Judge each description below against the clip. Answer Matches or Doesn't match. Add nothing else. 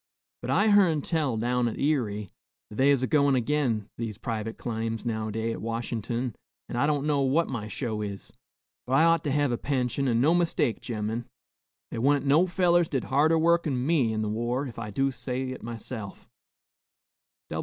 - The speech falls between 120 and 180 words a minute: Doesn't match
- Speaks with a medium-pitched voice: Doesn't match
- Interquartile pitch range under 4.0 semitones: Doesn't match